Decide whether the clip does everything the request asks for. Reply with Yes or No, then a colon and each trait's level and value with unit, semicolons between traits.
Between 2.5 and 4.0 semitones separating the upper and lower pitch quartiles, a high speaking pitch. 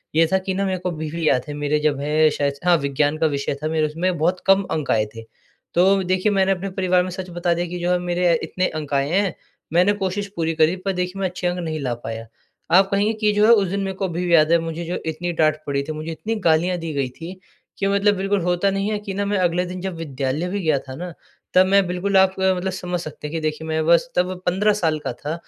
No: average, 3.3 semitones; medium, 175 Hz